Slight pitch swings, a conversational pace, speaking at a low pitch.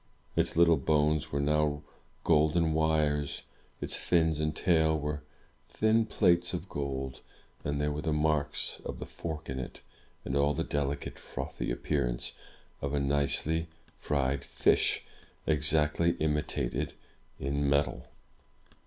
No: narrow, 1.8 semitones; slow, 130 wpm; very low, 75 Hz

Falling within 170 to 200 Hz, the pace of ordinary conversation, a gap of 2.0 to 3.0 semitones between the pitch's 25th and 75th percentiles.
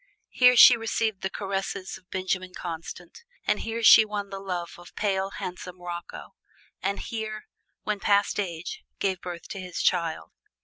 Yes: high, 190 Hz; average, 160 wpm; average, 2.7 semitones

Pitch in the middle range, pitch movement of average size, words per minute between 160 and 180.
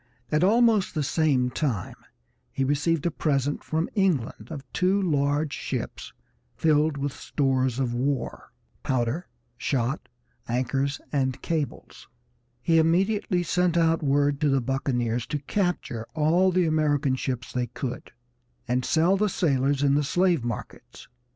No: medium, 145 Hz; average, 4.0 semitones; average, 140 wpm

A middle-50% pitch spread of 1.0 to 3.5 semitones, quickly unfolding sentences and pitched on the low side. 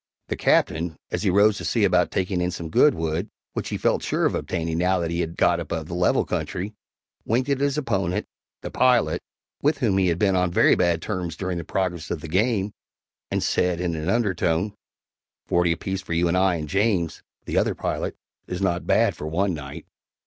Yes: average, 2.9 semitones; fast, 210 wpm; very low, 90 Hz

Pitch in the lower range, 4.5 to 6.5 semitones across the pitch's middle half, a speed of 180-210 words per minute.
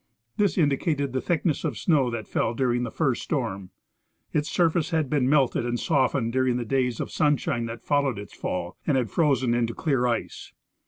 No: low, 130 Hz; average, 3.9 semitones; average, 190 wpm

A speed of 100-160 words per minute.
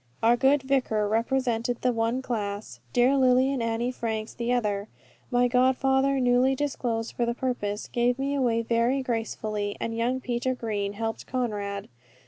Yes: average, 155 wpm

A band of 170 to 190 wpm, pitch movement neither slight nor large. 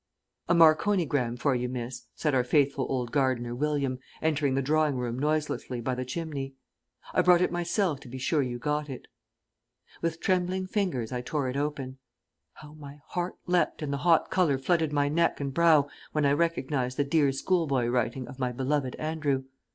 Yes: average, 180 wpm; average, 3.6 semitones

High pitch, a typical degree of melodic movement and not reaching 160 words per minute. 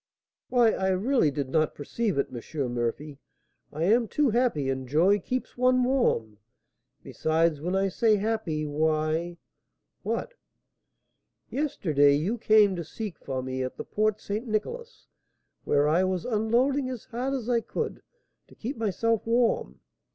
No: high, 195 Hz; wide, 7.4 semitones; average, 150 wpm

